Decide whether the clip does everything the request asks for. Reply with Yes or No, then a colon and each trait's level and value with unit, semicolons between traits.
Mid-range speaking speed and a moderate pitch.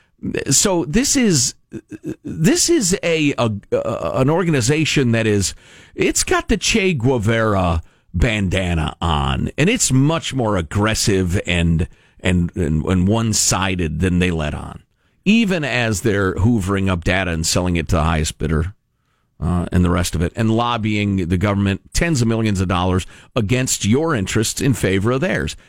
No: average, 160 wpm; low, 105 Hz